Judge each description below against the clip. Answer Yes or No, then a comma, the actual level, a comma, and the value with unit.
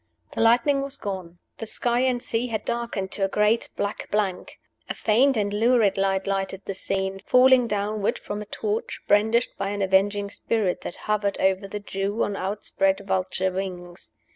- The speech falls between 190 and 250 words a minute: No, average, 175 wpm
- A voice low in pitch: No, high, 205 Hz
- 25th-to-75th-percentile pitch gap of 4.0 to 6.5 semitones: No, average, 2.8 semitones